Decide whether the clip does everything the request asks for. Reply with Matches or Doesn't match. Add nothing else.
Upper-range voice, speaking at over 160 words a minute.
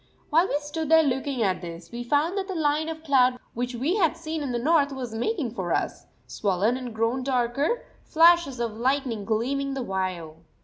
Matches